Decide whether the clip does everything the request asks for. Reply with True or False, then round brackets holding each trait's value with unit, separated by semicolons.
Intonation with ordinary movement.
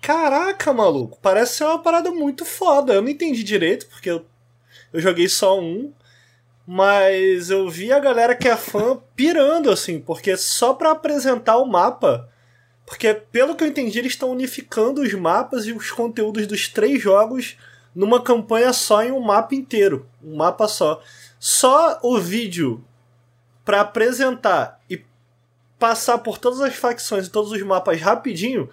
False (5.9 semitones)